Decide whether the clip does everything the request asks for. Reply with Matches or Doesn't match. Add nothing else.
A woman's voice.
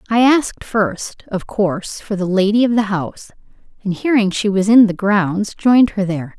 Matches